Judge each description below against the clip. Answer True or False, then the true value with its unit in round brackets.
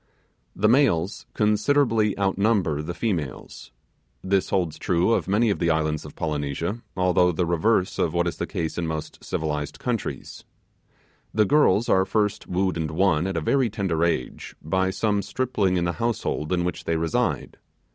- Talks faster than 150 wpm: True (165 wpm)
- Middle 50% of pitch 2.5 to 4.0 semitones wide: False (4.4 semitones)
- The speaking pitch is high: False (90 Hz)